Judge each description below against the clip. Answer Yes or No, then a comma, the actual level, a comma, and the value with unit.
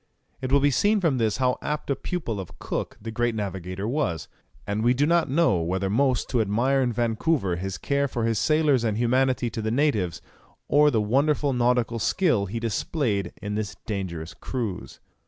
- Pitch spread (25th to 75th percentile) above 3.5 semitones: Yes, average, 5.3 semitones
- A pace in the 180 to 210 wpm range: Yes, average, 190 wpm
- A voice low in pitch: Yes, low, 120 Hz